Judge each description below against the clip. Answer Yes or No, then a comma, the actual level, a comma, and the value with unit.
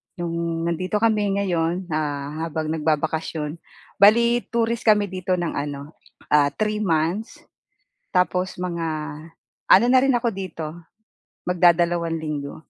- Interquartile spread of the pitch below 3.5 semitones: No, average, 4.1 semitones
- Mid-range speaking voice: Yes, medium, 170 Hz